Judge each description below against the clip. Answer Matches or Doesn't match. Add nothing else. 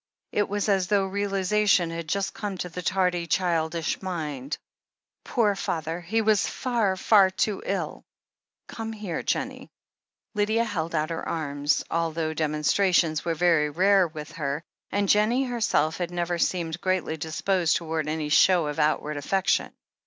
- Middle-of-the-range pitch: Matches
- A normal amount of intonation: Matches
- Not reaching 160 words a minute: Matches